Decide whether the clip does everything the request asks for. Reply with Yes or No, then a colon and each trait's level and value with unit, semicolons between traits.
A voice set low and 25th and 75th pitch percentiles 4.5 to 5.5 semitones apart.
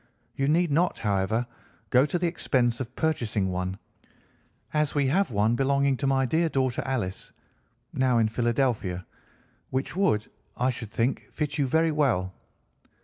Yes: low, 130 Hz; average, 4.8 semitones